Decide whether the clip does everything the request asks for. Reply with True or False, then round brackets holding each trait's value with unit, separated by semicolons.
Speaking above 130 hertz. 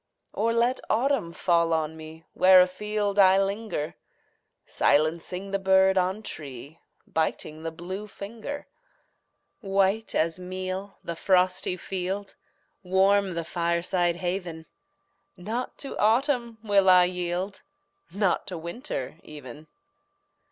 True (185 Hz)